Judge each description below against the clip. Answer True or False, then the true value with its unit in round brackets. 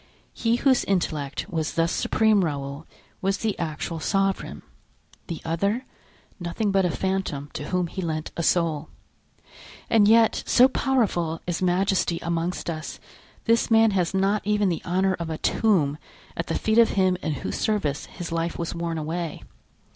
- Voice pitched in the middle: True (180 Hz)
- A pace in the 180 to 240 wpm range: False (160 wpm)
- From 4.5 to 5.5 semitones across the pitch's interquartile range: False (3.7 semitones)